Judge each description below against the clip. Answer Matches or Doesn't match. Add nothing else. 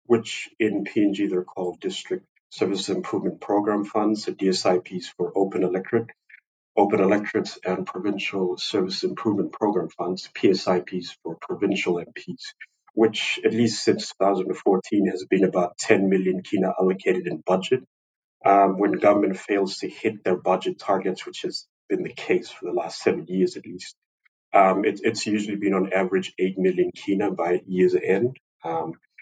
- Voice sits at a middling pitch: Doesn't match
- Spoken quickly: Doesn't match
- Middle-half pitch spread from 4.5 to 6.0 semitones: Doesn't match